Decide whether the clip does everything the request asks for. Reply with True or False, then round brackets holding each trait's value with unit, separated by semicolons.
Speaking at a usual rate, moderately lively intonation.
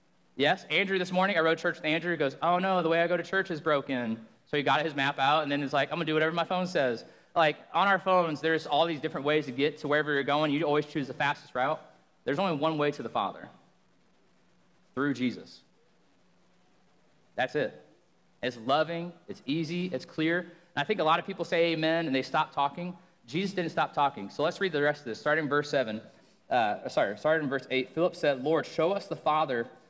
False (235 wpm; 3.1 semitones)